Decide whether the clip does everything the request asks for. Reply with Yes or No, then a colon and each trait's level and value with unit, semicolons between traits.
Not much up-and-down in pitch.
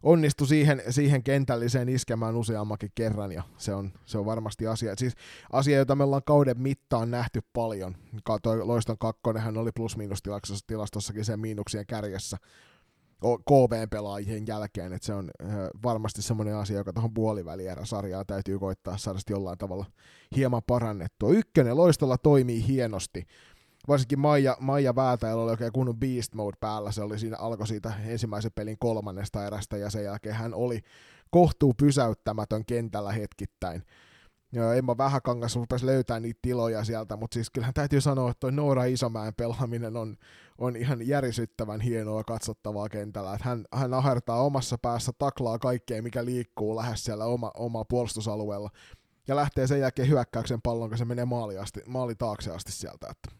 No: average, 3.0 semitones